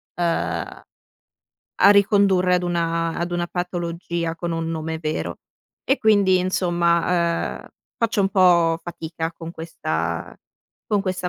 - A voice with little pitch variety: Yes, narrow, 2.0 semitones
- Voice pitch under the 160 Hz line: No, medium, 175 Hz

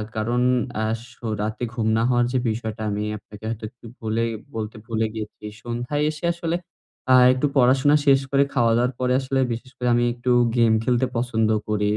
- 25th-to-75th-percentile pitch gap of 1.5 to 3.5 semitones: Yes, narrow, 2.5 semitones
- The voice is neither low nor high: No, low, 120 Hz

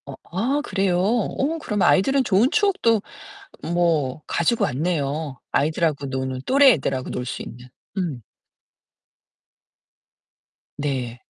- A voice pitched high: No, medium, 170 Hz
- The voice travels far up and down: Yes, wide, 8.7 semitones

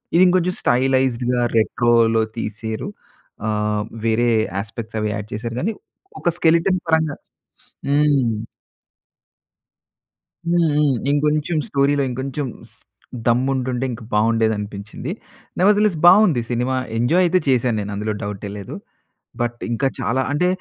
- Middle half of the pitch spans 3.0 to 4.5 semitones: No, average, 4.9 semitones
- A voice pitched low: Yes, low, 125 Hz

